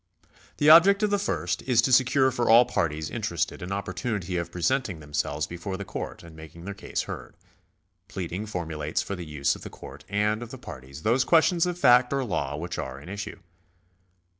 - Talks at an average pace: Yes, average, 195 wpm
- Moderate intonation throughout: No, wide, 7.2 semitones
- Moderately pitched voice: No, low, 100 Hz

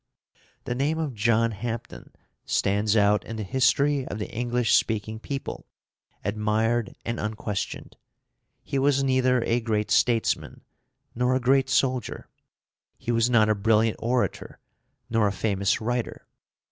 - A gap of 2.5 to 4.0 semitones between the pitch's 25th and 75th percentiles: Yes, average, 2.9 semitones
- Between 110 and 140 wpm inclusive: Yes, slow, 135 wpm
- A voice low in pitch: Yes, low, 115 Hz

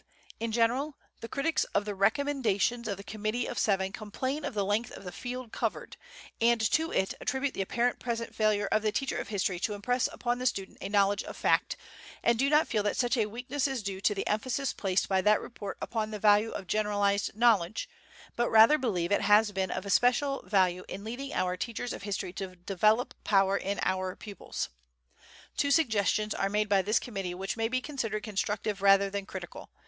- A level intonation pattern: No, average, 3.4 semitones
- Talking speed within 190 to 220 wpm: Yes, fast, 205 wpm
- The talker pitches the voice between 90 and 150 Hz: No, high, 215 Hz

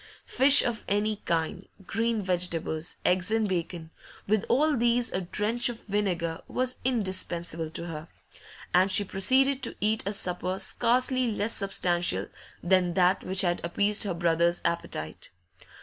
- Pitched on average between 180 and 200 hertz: Yes, high, 190 Hz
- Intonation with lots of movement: No, average, 4.5 semitones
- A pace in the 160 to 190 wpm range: No, average, 145 wpm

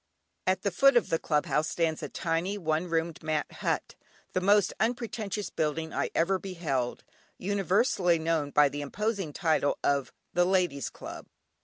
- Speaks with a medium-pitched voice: Yes, medium, 170 Hz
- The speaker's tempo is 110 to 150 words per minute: No, average, 160 wpm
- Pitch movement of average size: Yes, average, 3.9 semitones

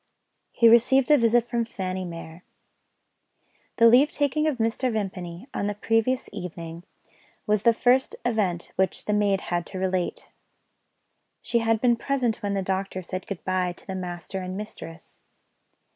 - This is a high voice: Yes, high, 205 Hz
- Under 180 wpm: Yes, average, 160 wpm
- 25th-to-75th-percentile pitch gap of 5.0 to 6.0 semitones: No, average, 4.2 semitones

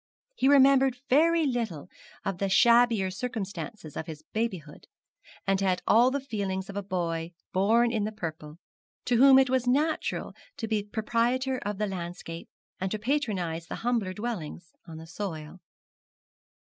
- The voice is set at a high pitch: Yes, high, 210 Hz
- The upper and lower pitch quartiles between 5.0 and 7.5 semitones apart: Yes, average, 5.3 semitones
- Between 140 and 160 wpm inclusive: Yes, average, 155 wpm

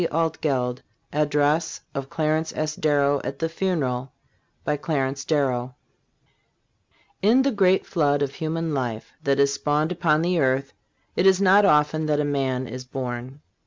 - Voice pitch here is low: No, medium, 145 Hz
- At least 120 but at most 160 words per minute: Yes, slow, 135 wpm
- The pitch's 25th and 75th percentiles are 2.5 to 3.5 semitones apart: Yes, average, 3.1 semitones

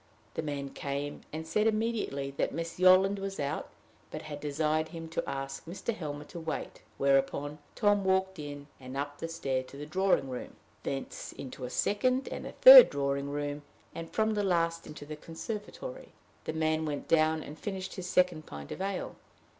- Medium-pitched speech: Yes, medium, 160 Hz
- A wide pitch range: No, average, 4.8 semitones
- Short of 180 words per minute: No, average, 185 wpm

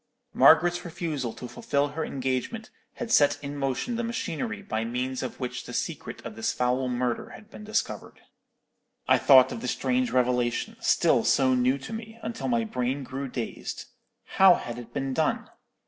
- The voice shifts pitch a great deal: Yes, wide, 7.2 semitones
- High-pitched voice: No, low, 135 Hz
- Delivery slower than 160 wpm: No, average, 175 wpm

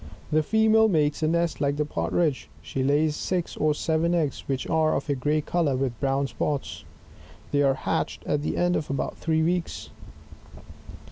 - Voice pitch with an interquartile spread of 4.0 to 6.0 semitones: No, average, 3.0 semitones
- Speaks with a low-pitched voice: No, medium, 150 Hz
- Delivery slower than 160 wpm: No, average, 180 wpm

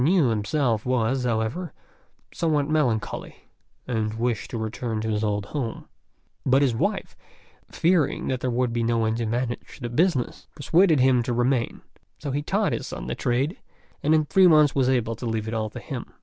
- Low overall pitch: Yes, low, 125 Hz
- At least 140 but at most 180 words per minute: No, average, 190 wpm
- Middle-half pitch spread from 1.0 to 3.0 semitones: No, average, 4.4 semitones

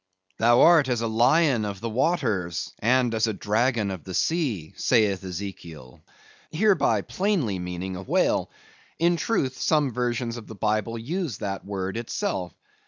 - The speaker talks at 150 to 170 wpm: Yes, average, 155 wpm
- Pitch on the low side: Yes, low, 115 Hz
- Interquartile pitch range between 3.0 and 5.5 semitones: Yes, average, 5.1 semitones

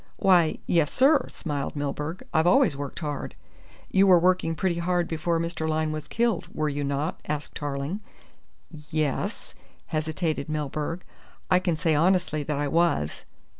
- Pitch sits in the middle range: Yes, medium, 160 Hz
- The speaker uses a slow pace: No, average, 155 wpm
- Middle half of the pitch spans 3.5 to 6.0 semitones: No, average, 3.1 semitones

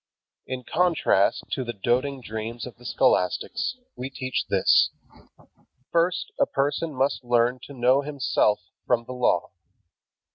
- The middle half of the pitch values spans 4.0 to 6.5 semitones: No, average, 2.8 semitones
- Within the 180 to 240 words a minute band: No, slow, 135 wpm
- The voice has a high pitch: No, low, 130 Hz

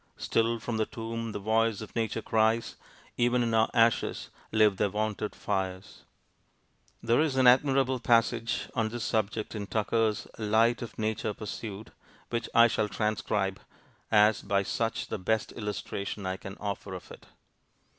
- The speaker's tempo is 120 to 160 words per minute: Yes, average, 155 wpm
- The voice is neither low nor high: No, low, 110 Hz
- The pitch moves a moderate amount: No, narrow, 1.8 semitones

